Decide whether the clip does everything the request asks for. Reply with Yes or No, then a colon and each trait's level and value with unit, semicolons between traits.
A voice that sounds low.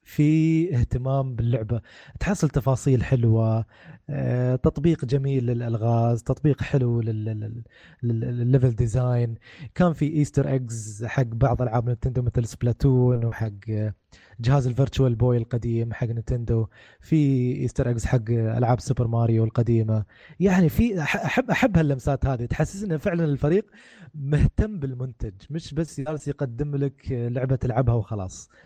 Yes: low, 125 Hz